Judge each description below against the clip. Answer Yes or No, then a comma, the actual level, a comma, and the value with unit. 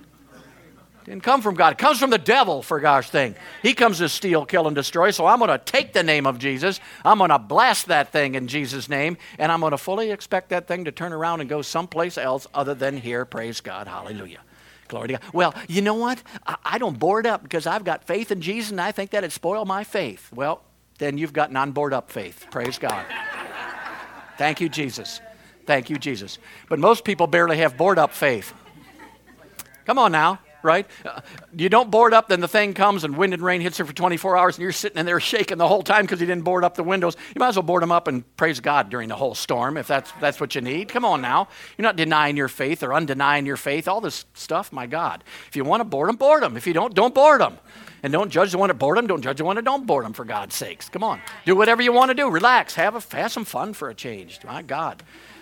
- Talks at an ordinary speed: No, fast, 250 wpm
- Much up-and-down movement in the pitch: Yes, wide, 5.7 semitones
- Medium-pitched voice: Yes, medium, 175 Hz